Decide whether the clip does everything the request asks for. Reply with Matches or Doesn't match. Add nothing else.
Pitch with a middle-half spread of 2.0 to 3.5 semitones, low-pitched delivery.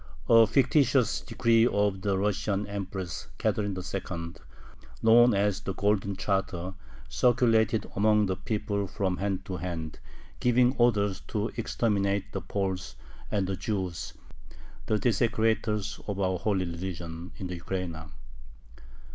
Matches